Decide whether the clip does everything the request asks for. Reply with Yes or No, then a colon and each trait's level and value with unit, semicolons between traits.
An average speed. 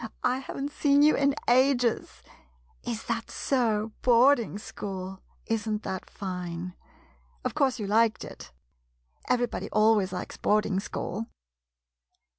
No: slow, 120 wpm